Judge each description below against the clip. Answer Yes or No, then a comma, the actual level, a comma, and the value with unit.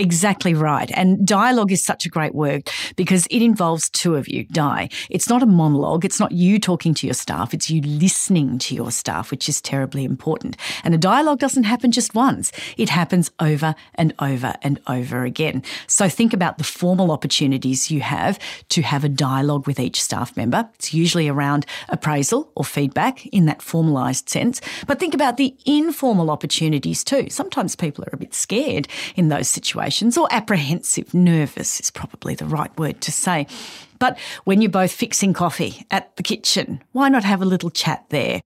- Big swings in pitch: Yes, wide, 5.8 semitones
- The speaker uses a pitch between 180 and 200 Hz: No, medium, 170 Hz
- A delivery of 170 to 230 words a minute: Yes, average, 185 wpm